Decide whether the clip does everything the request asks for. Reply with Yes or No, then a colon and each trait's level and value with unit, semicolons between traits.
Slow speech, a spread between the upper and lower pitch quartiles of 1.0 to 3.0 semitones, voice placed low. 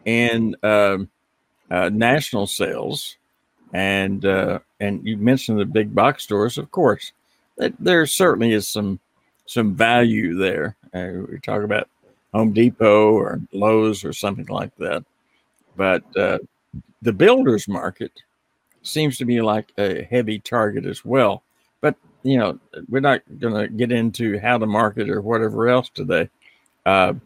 No: average, 145 wpm; average, 2.7 semitones; low, 110 Hz